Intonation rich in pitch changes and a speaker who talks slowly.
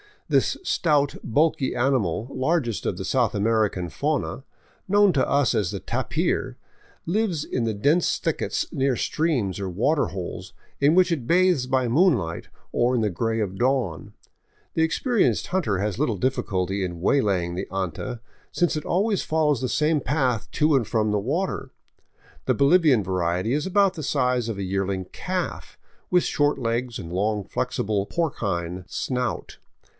No: wide, 7.3 semitones; average, 160 wpm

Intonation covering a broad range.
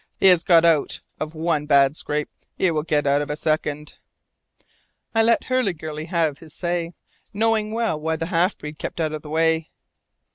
No: narrow, 2.6 semitones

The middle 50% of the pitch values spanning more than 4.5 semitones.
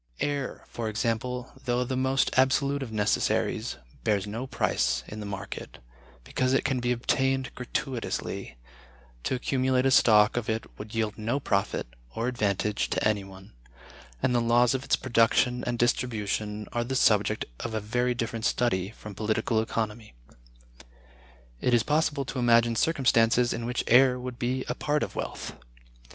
No: average, 2.9 semitones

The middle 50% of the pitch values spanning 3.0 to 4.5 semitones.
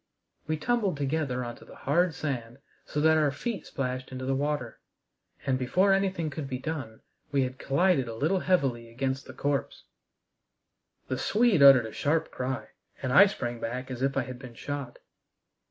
Yes: average, 3.8 semitones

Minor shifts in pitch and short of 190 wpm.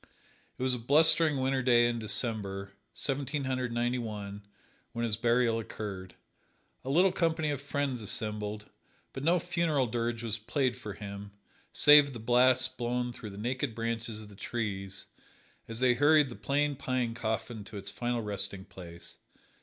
No: average, 3.7 semitones; average, 160 wpm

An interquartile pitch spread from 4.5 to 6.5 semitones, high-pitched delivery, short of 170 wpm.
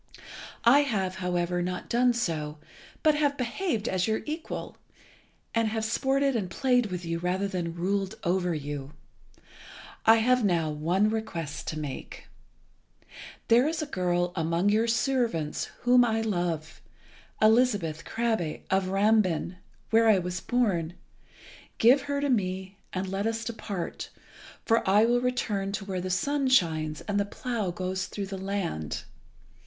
Yes: average, 4.8 semitones; high, 200 Hz; average, 150 wpm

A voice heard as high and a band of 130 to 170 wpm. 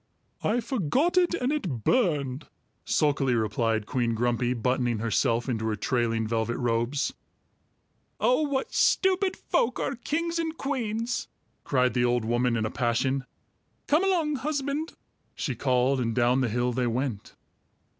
No: low, 130 Hz; average, 145 wpm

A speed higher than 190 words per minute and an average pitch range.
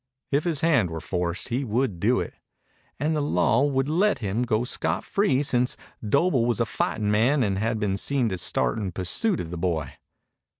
No: average, 200 wpm; wide, 6.6 semitones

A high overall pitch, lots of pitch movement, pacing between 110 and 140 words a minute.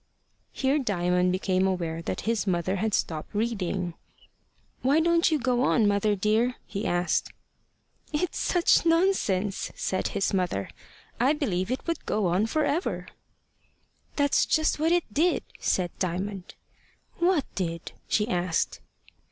Yes: high, 210 Hz; wide, 7.7 semitones; slow, 135 wpm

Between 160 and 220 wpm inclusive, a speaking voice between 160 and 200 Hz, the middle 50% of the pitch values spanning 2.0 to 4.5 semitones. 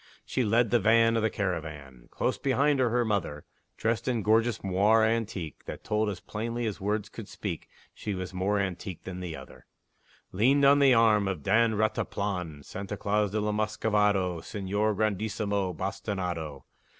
No: average, 165 wpm; low, 105 Hz; average, 3.2 semitones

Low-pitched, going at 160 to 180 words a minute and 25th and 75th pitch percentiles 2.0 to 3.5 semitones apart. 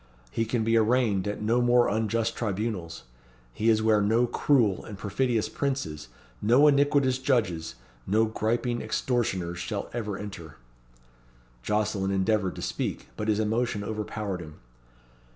No: low, 110 Hz; slow, 135 wpm; average, 3.0 semitones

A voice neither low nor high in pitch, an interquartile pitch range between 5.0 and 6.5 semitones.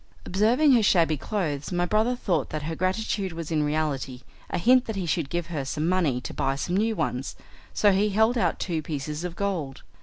Yes: medium, 175 Hz; wide, 5.4 semitones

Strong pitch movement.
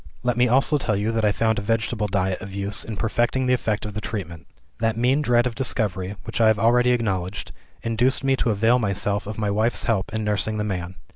No: average, 2.8 semitones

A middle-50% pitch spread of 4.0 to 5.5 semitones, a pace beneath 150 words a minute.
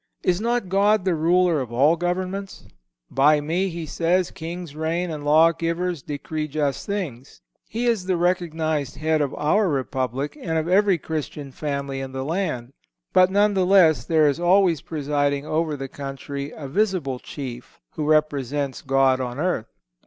No: average, 4.3 semitones; average, 155 wpm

